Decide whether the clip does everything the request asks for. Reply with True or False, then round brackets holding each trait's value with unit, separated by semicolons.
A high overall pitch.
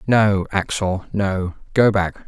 False (100 Hz)